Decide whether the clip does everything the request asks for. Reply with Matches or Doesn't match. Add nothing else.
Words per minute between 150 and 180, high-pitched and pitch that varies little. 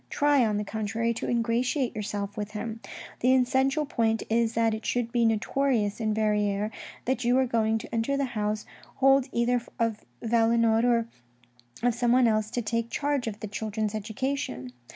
Matches